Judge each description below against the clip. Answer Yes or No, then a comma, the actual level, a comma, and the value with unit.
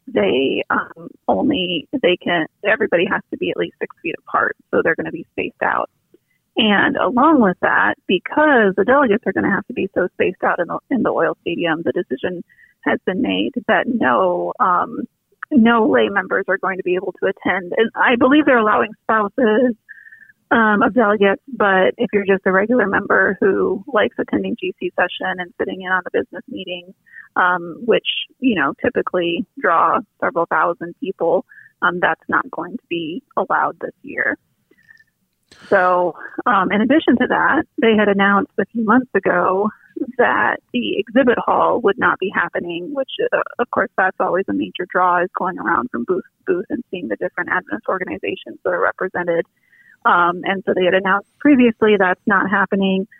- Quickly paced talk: No, average, 185 wpm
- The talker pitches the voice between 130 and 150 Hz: No, high, 215 Hz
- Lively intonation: Yes, wide, 7.5 semitones